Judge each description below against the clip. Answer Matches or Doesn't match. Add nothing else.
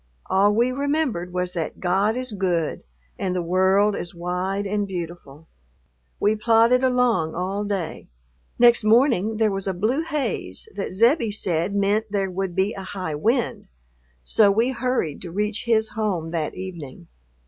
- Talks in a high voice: Matches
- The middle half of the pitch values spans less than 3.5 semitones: Doesn't match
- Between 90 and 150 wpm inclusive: Doesn't match